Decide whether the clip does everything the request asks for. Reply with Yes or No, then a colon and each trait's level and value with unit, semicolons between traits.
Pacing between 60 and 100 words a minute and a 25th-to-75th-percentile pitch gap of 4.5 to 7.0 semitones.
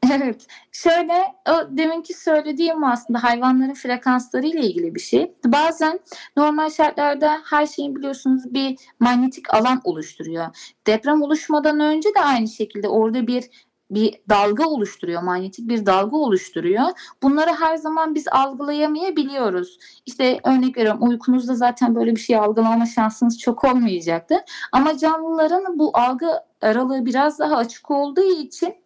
No: average, 130 wpm; average, 5.0 semitones